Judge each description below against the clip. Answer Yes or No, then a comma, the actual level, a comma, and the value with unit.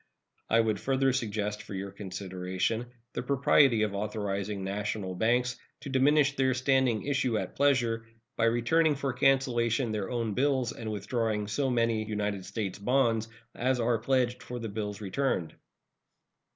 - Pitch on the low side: Yes, low, 115 Hz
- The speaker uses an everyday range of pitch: Yes, average, 4.0 semitones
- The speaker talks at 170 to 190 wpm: No, average, 150 wpm